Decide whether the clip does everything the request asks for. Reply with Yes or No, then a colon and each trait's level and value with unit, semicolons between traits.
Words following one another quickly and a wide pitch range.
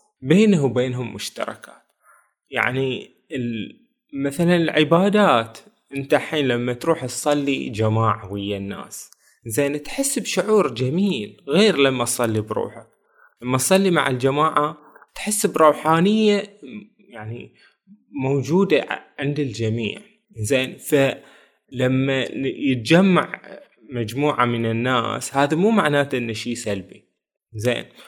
No: average, 95 wpm; wide, 7.0 semitones